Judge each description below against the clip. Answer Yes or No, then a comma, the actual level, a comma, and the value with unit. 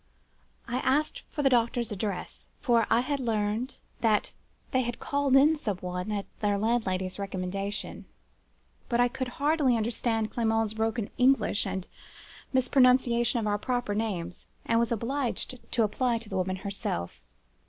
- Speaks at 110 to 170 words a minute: Yes, average, 150 wpm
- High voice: Yes, high, 230 Hz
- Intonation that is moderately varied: Yes, average, 3.5 semitones